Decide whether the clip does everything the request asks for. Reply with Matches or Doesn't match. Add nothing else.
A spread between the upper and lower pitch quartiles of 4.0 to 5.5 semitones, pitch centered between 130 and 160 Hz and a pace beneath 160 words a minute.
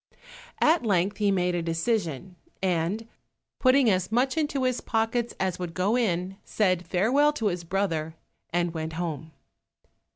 Doesn't match